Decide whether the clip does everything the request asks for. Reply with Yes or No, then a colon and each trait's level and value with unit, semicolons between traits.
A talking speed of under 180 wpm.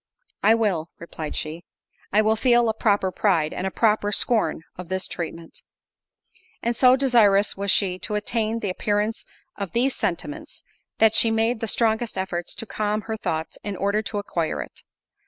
Yes: average, 170 wpm